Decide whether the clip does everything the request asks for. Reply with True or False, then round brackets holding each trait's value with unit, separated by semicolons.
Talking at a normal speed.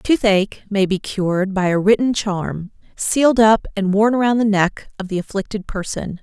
True (185 wpm)